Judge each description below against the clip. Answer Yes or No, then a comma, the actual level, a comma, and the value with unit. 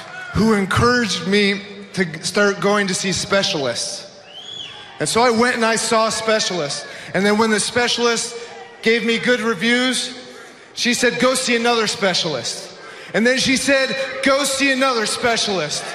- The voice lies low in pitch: No, high, 225 Hz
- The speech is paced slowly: No, average, 150 wpm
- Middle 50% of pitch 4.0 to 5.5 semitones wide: No, average, 3.6 semitones